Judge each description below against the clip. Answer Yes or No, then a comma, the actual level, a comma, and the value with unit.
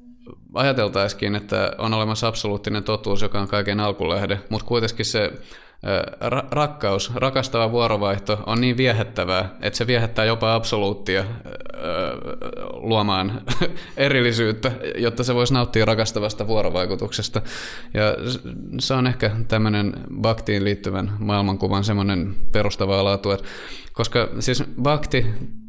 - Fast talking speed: No, average, 110 wpm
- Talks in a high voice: No, low, 110 Hz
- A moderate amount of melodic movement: Yes, average, 3.1 semitones